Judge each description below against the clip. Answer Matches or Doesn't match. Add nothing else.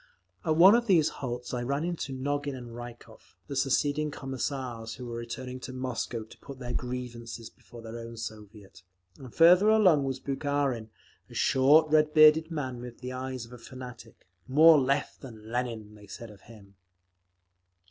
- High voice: Doesn't match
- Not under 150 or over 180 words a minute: Matches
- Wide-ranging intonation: Doesn't match